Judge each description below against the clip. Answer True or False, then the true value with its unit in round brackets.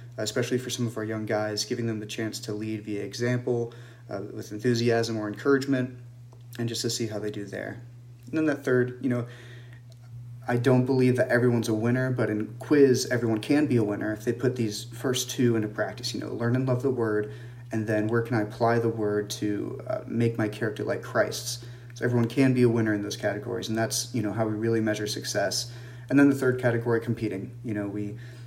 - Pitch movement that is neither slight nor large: False (2.1 semitones)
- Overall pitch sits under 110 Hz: False (120 Hz)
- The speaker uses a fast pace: True (225 wpm)